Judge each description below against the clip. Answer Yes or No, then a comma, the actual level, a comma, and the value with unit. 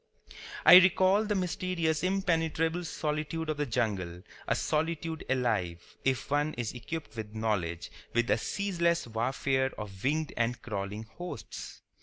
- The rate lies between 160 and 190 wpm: No, slow, 135 wpm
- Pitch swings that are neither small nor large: No, wide, 6.9 semitones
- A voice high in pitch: No, medium, 145 Hz